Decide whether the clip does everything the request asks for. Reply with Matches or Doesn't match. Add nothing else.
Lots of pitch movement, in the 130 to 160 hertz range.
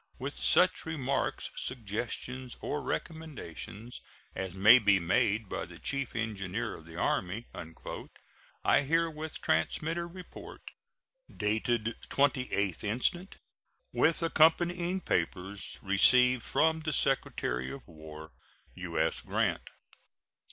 Doesn't match